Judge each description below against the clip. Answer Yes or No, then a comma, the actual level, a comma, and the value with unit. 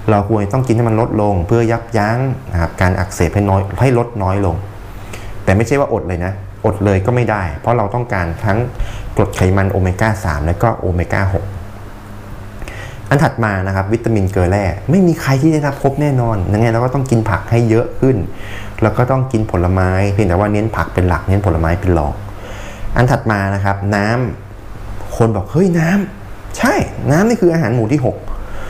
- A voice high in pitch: No, low, 105 Hz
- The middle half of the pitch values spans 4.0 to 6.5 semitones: No, average, 3.2 semitones